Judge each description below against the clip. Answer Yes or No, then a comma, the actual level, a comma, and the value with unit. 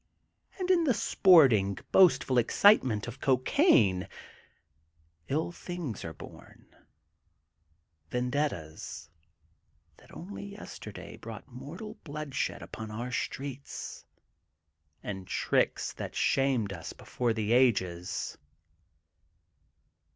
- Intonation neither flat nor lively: No, wide, 6.9 semitones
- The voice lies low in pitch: Yes, low, 125 Hz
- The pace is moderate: No, slow, 90 wpm